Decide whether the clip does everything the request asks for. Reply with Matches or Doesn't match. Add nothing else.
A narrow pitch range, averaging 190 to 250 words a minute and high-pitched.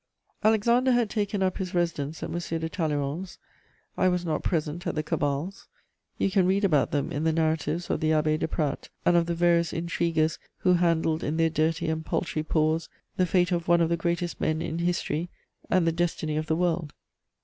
Doesn't match